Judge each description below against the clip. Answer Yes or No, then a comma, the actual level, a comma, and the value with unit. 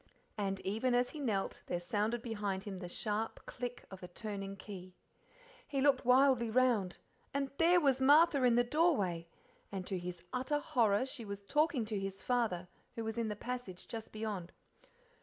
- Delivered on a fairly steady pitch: No, average, 4.7 semitones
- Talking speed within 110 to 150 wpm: No, average, 175 wpm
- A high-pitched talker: Yes, high, 225 Hz